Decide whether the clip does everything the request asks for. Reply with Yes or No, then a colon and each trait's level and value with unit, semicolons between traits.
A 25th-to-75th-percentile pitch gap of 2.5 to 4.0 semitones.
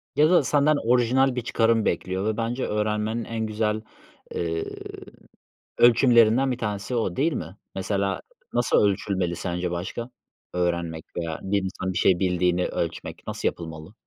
No: average, 4.6 semitones